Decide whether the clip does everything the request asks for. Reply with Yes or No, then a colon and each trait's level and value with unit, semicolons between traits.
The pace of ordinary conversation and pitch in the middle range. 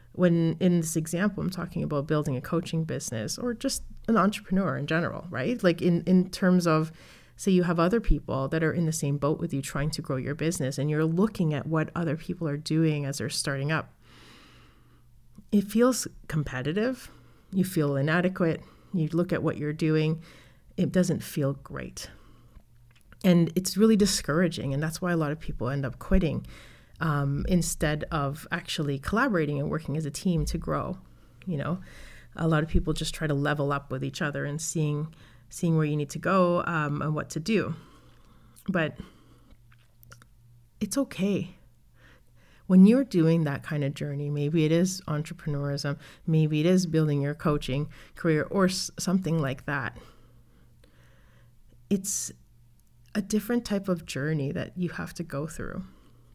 Yes: average, 170 wpm; medium, 155 Hz